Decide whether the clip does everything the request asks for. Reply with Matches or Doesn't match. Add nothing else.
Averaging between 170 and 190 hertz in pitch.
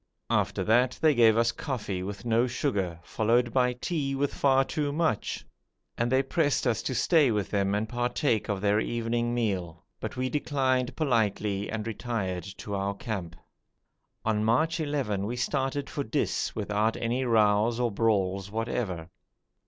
Doesn't match